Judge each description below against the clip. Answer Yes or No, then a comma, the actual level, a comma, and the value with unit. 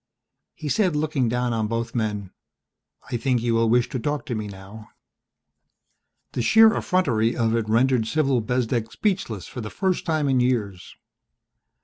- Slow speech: No, average, 160 wpm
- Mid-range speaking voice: No, low, 120 Hz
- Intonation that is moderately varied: Yes, average, 3.9 semitones